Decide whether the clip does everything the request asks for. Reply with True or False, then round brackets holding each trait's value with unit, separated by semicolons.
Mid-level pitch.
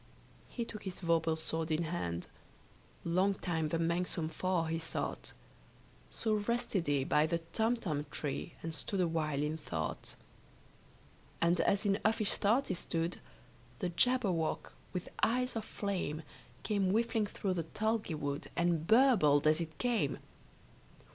True (170 Hz)